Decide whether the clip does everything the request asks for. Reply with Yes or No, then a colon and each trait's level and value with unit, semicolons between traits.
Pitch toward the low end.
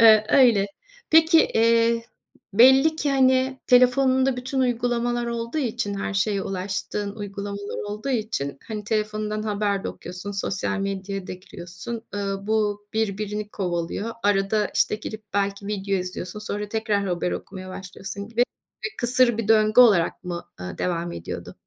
No: high, 210 Hz